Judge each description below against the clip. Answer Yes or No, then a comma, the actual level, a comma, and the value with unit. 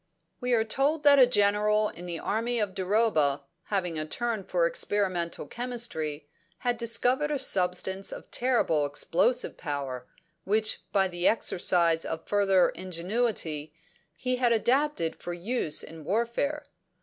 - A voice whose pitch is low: No, high, 205 Hz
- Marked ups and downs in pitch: Yes, wide, 6.0 semitones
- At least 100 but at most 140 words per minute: Yes, slow, 135 wpm